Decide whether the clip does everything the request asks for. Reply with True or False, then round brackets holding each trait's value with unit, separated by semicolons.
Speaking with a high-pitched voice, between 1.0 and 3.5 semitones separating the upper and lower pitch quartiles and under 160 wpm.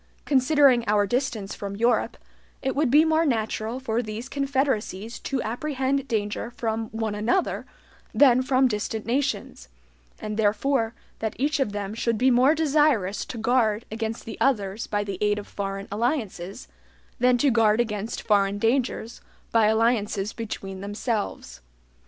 False (225 Hz; 3.9 semitones; 145 wpm)